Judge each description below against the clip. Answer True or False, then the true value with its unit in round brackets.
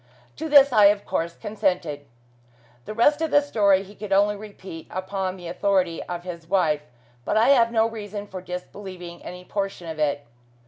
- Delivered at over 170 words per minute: True (180 wpm)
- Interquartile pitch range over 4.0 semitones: False (3.3 semitones)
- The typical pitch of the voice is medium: False (195 Hz)